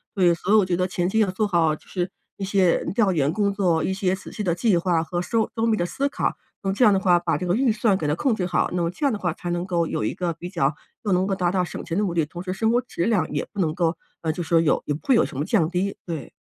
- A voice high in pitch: No, medium, 180 Hz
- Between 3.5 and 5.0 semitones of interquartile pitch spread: No, average, 3.0 semitones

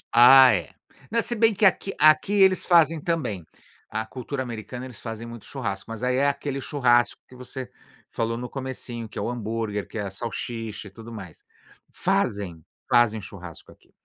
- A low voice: Yes, low, 120 Hz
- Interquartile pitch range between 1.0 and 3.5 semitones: No, average, 3.9 semitones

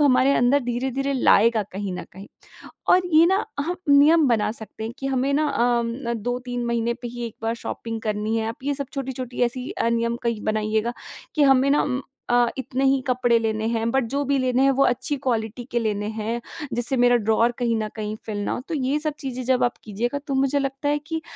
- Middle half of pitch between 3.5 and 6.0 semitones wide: No, average, 3.1 semitones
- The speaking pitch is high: Yes, high, 245 Hz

